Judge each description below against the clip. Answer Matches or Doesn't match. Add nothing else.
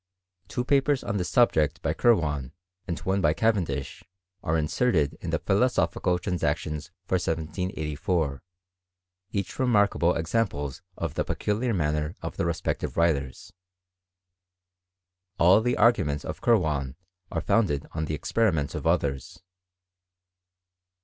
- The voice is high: Doesn't match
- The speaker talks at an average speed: Doesn't match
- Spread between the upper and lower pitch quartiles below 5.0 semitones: Doesn't match